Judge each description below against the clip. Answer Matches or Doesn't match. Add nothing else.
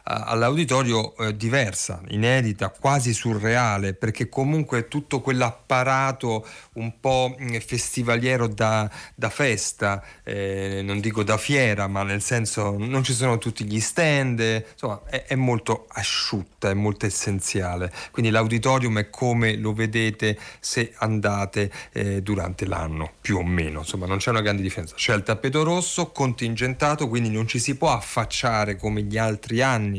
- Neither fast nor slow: Matches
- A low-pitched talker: Matches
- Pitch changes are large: Doesn't match